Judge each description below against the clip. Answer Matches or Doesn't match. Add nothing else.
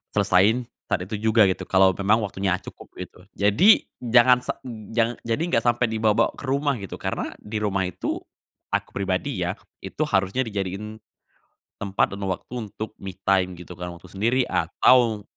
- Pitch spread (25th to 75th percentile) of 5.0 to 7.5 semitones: Doesn't match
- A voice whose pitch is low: Matches